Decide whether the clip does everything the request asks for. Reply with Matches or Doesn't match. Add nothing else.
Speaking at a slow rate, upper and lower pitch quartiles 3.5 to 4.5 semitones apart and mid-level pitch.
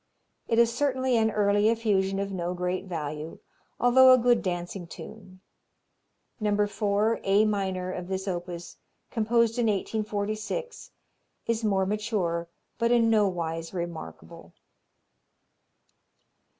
Doesn't match